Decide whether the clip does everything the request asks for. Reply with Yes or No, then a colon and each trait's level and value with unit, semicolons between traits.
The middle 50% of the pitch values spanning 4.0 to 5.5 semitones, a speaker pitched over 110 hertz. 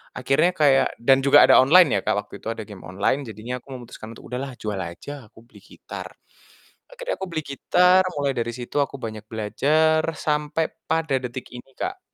Yes: average, 5.2 semitones; low, 135 Hz